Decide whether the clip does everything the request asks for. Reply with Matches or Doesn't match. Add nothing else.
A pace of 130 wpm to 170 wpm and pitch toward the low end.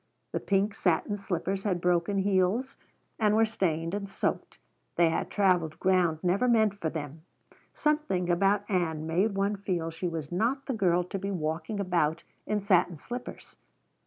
Doesn't match